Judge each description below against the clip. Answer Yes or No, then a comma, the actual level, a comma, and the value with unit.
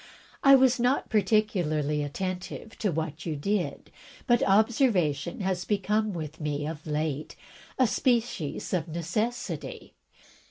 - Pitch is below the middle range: No, medium, 185 Hz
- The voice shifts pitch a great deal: Yes, wide, 6.1 semitones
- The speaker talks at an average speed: No, slow, 120 wpm